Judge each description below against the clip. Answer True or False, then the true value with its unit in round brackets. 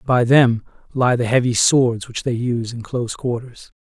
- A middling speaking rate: True (190 wpm)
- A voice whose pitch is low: True (120 Hz)